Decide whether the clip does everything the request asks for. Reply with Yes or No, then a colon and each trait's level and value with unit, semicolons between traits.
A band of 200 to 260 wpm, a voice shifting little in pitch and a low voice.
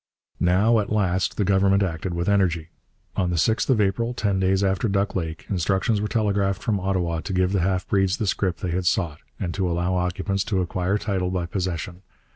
Yes: fast, 205 wpm; narrow, 2.0 semitones; very low, 95 Hz